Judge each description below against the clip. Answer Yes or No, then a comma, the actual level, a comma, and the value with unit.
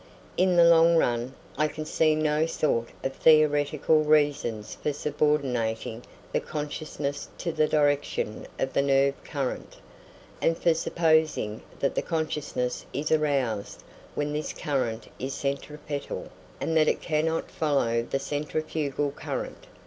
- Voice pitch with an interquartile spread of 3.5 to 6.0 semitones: No, narrow, 2.4 semitones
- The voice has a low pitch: No, medium, 150 Hz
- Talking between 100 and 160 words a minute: Yes, slow, 135 wpm